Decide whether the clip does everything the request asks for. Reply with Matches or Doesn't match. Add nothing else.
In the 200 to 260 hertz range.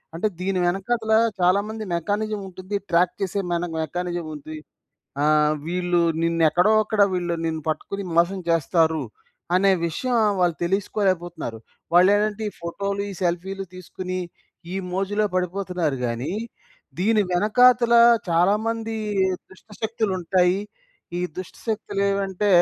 Doesn't match